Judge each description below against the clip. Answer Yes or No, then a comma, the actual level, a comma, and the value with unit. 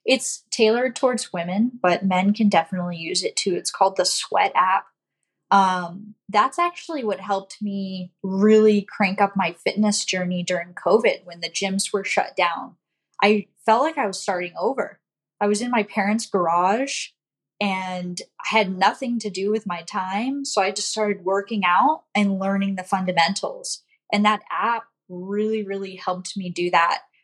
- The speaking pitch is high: Yes, high, 200 Hz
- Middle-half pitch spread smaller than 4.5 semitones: Yes, average, 2.8 semitones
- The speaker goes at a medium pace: Yes, average, 170 wpm